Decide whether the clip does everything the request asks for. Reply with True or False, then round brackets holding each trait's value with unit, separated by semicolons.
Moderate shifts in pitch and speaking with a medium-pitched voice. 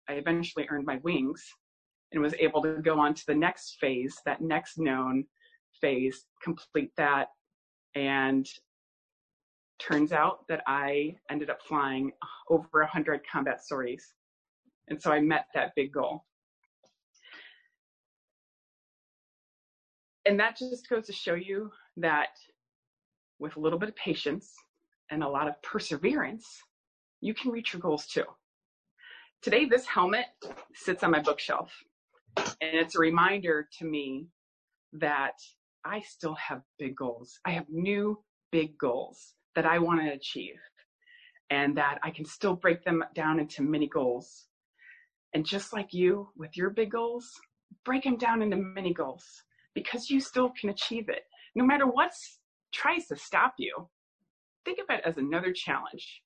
False (6.9 semitones; 165 Hz)